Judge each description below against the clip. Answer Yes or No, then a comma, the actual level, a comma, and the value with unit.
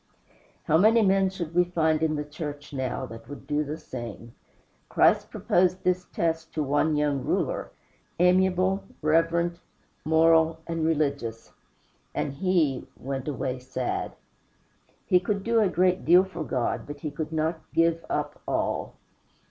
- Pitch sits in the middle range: Yes, medium, 160 Hz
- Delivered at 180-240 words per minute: No, average, 150 wpm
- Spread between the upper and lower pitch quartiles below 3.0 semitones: No, average, 3.6 semitones